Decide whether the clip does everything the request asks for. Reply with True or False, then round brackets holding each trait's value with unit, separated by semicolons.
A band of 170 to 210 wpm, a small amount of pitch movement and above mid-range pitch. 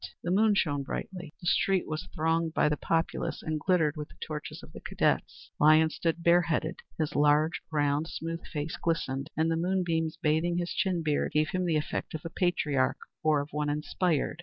False (190 wpm; 2.3 semitones; 160 Hz)